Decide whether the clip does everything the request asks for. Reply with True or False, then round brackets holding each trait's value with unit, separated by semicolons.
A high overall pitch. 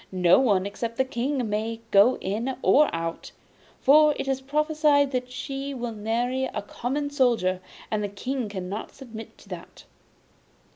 True (245 Hz)